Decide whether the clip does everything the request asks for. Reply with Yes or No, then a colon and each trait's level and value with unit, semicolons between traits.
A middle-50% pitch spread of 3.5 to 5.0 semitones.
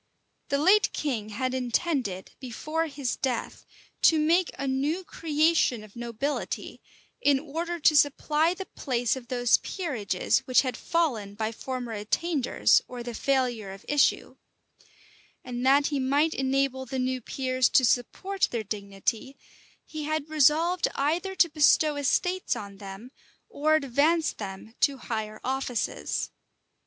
Yes: average, 4.5 semitones